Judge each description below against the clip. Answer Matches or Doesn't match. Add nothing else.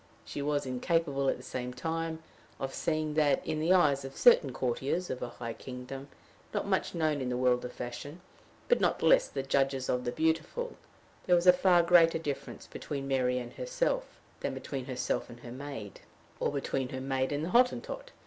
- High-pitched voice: Doesn't match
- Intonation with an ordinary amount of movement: Matches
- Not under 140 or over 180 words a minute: Doesn't match